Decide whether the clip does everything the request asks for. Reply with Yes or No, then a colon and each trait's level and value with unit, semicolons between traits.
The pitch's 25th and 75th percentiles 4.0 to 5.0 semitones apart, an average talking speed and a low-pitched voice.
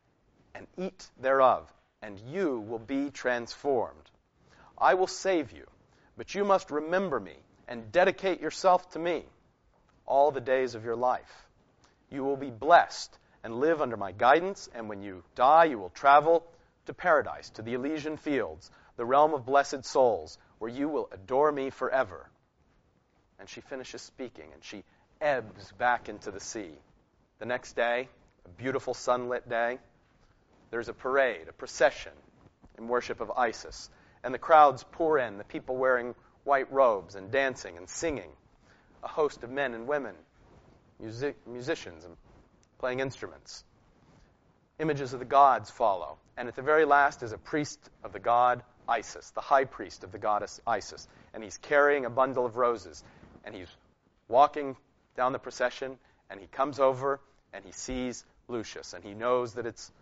No: average, 3.5 semitones; average, 165 wpm; low, 130 Hz